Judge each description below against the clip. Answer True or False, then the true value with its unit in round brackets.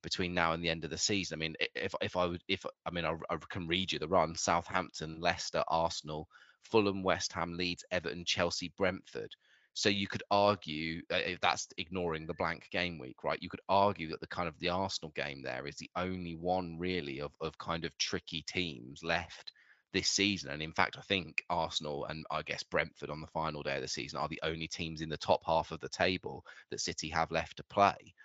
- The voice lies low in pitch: True (85 Hz)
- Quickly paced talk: True (225 wpm)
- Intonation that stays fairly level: True (2.2 semitones)